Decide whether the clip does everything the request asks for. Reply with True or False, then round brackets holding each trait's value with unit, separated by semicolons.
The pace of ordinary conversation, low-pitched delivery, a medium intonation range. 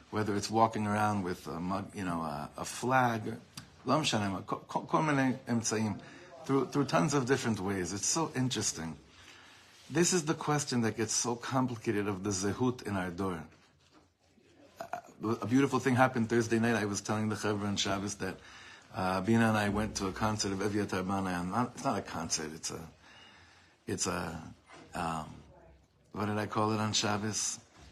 True (165 wpm; 105 Hz; 3.7 semitones)